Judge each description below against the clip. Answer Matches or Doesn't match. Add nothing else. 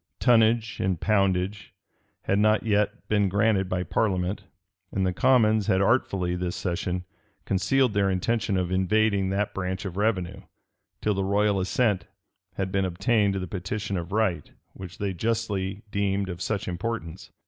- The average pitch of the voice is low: Matches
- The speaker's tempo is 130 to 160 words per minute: Matches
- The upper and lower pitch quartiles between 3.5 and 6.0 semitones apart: Doesn't match